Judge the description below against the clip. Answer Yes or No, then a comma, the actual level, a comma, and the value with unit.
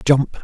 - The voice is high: No, low, 135 Hz